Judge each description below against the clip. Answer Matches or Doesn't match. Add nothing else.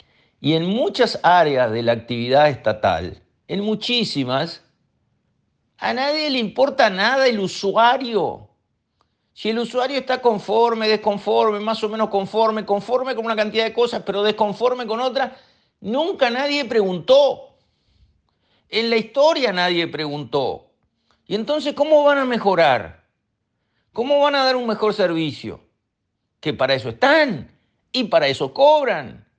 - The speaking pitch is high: Matches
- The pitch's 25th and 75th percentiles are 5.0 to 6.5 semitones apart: Matches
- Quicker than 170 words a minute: Doesn't match